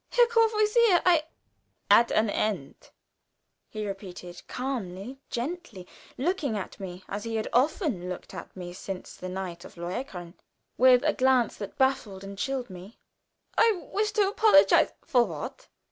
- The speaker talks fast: No, average, 155 wpm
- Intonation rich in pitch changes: Yes, wide, 8.5 semitones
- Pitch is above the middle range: Yes, high, 230 Hz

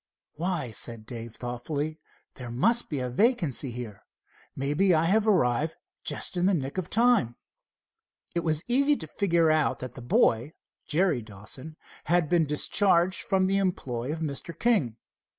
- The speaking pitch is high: No, medium, 155 Hz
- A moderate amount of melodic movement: No, wide, 7.0 semitones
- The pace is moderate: Yes, average, 155 wpm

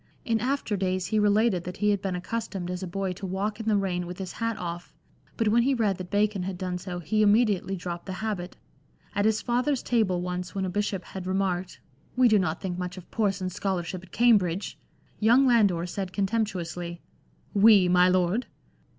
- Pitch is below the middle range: No, high, 195 Hz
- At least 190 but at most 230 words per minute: Yes, average, 200 wpm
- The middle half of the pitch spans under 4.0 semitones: Yes, average, 3.0 semitones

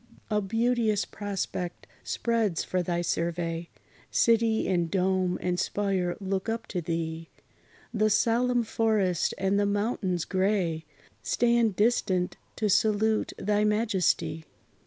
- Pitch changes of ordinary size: Yes, average, 3.6 semitones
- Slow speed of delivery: Yes, slow, 115 wpm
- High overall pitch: Yes, high, 200 Hz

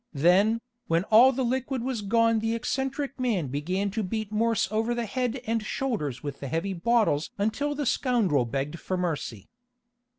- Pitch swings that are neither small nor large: No, wide, 6.0 semitones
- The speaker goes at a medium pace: Yes, average, 170 wpm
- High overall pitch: Yes, high, 220 Hz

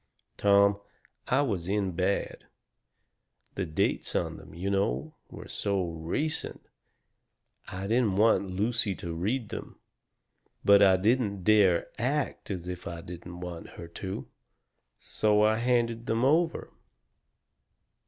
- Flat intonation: No, average, 4.0 semitones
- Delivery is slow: Yes, slow, 130 wpm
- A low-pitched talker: Yes, low, 100 Hz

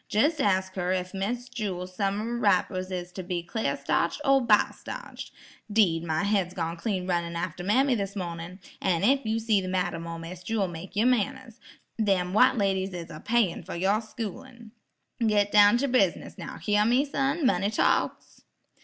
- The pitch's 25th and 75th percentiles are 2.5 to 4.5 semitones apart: Yes, average, 3.9 semitones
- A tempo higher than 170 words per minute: Yes, average, 180 wpm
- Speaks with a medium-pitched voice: No, high, 195 Hz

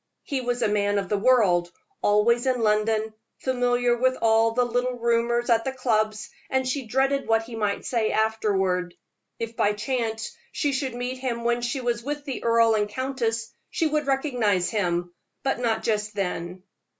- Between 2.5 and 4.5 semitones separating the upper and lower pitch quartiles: Yes, average, 3.0 semitones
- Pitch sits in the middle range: No, high, 230 Hz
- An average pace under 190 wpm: Yes, average, 175 wpm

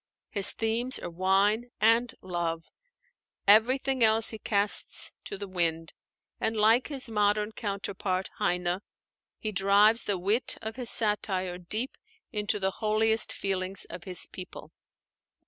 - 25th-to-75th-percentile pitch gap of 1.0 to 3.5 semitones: Yes, average, 3.0 semitones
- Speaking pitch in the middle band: No, high, 205 Hz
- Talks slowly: Yes, slow, 130 wpm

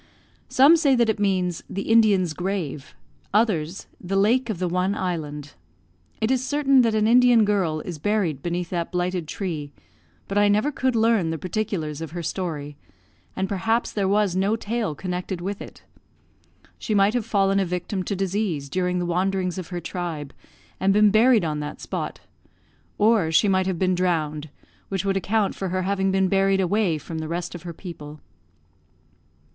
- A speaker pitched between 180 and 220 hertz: Yes, high, 190 Hz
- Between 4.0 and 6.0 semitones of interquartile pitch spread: No, average, 3.5 semitones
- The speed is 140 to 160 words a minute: No, average, 180 wpm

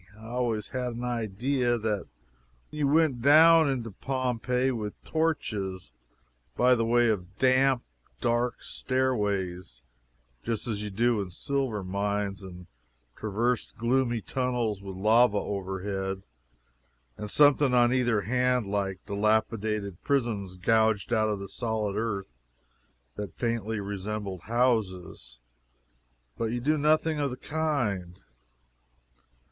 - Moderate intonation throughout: Yes, average, 4.0 semitones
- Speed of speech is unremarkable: No, slow, 120 wpm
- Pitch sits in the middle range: No, low, 115 Hz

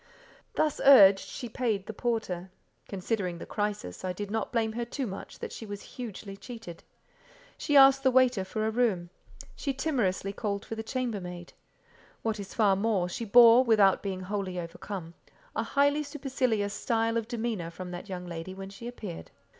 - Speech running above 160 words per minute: Yes, average, 175 wpm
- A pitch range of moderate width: Yes, average, 4.1 semitones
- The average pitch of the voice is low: No, high, 215 Hz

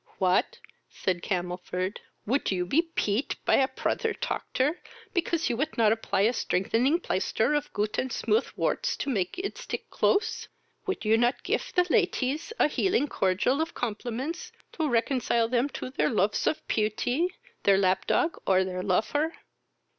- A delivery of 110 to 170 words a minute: Yes, average, 160 wpm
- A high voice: Yes, high, 245 Hz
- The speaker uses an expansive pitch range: Yes, wide, 7.8 semitones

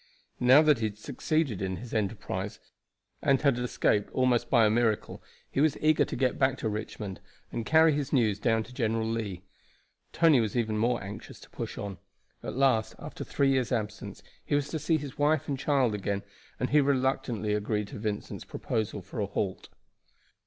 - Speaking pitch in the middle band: No, low, 115 Hz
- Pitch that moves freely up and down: No, average, 4.4 semitones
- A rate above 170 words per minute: Yes, average, 190 wpm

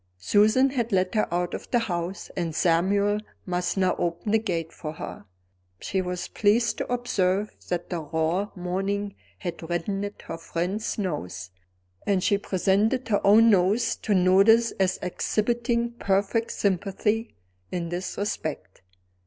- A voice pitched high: Yes, high, 195 Hz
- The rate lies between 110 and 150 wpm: Yes, average, 145 wpm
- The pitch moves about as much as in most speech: Yes, average, 3.2 semitones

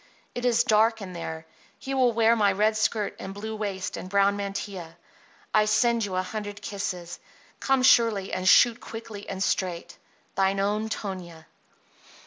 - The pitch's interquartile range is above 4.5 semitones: No, average, 2.8 semitones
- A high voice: Yes, high, 205 Hz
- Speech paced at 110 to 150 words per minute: No, average, 160 wpm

